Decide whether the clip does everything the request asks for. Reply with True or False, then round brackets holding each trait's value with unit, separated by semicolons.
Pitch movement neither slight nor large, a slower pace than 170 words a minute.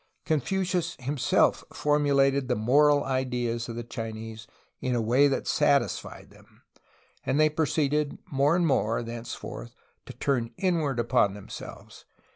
True (4.0 semitones; 135 wpm)